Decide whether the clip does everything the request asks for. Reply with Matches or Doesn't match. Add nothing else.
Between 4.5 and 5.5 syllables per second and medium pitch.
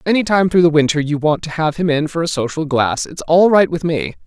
Doesn't match